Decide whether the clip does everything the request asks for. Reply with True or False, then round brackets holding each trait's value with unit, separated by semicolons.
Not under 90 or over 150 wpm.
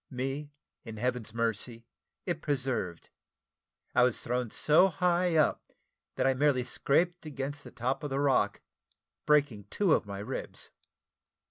True (140 wpm)